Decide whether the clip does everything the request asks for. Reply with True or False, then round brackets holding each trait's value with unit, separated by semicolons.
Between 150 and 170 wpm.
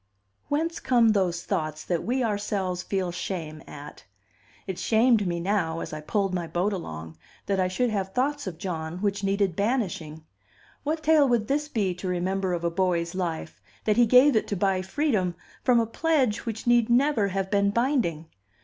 False (185 wpm)